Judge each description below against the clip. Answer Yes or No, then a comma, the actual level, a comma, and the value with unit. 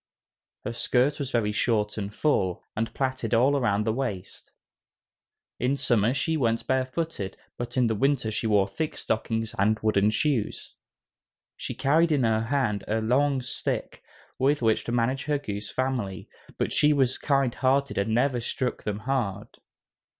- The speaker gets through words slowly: No, average, 155 wpm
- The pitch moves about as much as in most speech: Yes, average, 4.0 semitones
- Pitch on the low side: Yes, low, 120 Hz